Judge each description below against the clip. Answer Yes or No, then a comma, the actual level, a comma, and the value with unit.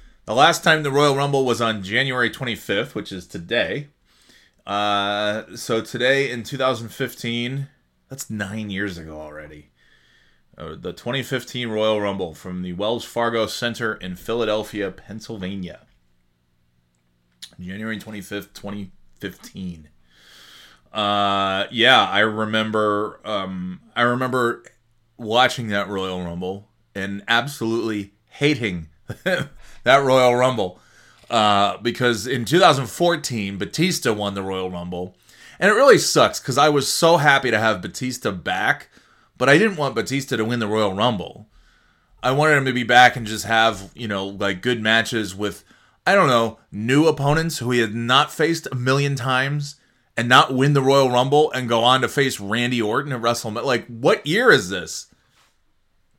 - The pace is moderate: Yes, average, 150 wpm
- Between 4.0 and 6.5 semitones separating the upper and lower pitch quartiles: Yes, average, 4.5 semitones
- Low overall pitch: Yes, low, 115 Hz